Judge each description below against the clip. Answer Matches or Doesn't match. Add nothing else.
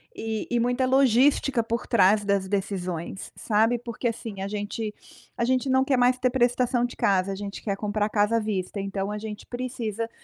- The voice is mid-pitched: Doesn't match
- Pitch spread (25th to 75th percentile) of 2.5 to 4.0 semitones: Matches